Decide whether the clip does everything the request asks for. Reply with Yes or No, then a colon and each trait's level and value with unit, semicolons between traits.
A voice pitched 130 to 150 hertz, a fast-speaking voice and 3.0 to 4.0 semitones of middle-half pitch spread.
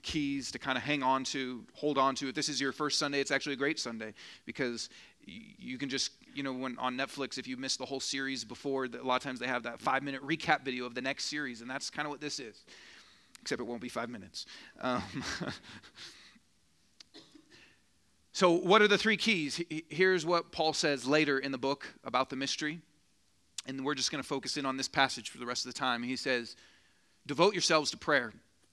No: low, 135 Hz; fast, 220 wpm; narrow, 2.6 semitones